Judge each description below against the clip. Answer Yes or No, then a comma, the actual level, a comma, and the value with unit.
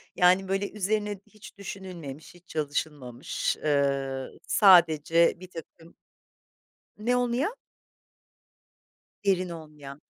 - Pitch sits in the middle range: Yes, medium, 175 Hz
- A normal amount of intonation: Yes, average, 4.7 semitones